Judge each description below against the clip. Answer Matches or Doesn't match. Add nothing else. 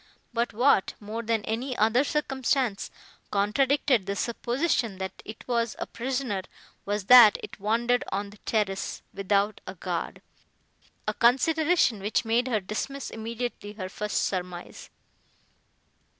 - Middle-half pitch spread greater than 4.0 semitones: Doesn't match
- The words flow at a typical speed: Doesn't match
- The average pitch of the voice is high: Matches